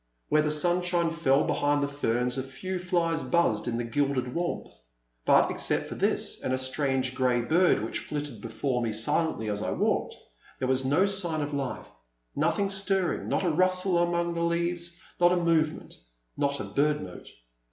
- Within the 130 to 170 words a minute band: No, average, 185 wpm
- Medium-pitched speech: Yes, medium, 150 Hz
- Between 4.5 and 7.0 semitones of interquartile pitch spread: Yes, average, 4.9 semitones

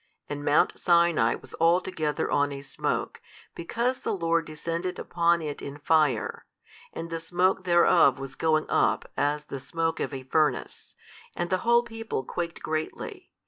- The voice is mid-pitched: Yes, medium, 165 Hz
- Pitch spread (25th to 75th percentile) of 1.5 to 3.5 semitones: Yes, average, 3.0 semitones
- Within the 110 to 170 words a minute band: Yes, average, 155 wpm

